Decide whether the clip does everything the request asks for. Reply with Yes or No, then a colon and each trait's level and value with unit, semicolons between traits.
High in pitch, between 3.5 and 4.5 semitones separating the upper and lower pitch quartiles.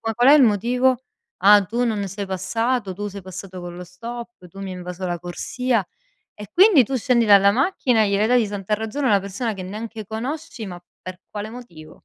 Yes: high, 210 Hz; average, 4.1 semitones